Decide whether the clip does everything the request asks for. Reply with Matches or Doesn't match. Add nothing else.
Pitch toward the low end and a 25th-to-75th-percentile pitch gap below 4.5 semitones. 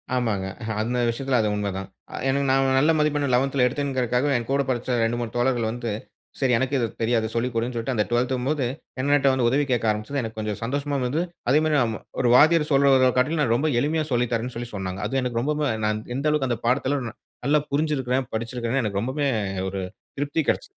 Matches